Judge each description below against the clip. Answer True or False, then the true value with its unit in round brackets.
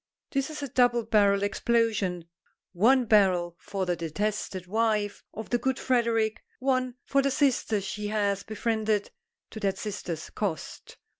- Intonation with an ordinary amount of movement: True (3.2 semitones)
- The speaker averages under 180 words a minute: True (145 wpm)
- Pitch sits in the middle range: False (215 Hz)